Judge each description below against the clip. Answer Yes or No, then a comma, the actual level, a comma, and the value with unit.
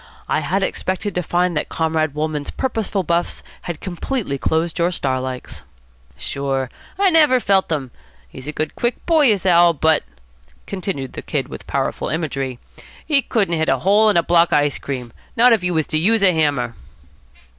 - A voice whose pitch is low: No, medium, 170 Hz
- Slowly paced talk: No, average, 185 wpm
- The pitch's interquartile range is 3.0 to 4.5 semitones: No, average, 5.1 semitones